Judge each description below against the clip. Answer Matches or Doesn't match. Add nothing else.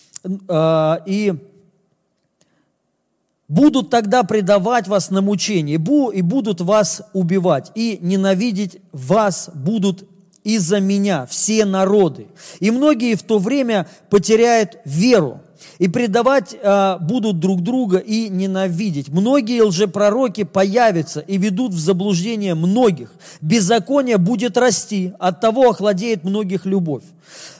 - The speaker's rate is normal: Doesn't match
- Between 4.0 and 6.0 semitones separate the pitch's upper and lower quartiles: Doesn't match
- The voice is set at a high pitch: Matches